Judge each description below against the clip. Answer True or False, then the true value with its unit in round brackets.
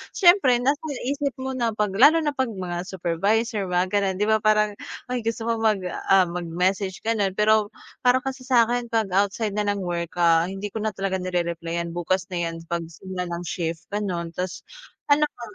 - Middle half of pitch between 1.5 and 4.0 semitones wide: False (4.4 semitones)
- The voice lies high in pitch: True (200 Hz)